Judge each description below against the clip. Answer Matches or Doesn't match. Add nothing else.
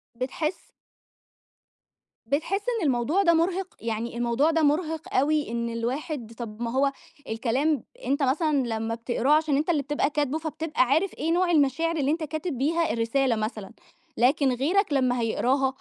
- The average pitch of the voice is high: Matches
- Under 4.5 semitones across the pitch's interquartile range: Doesn't match